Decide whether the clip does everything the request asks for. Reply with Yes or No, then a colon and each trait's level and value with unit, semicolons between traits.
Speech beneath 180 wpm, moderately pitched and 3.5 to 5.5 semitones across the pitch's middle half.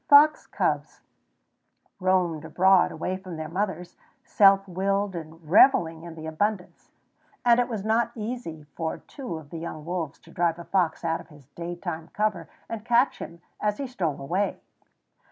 Yes: average, 165 wpm; medium, 180 Hz; average, 4.2 semitones